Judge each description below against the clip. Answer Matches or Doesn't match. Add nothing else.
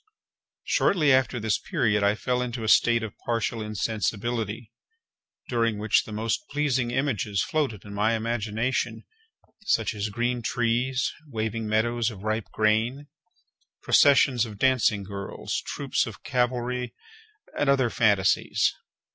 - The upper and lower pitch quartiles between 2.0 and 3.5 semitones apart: Matches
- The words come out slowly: Matches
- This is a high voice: Doesn't match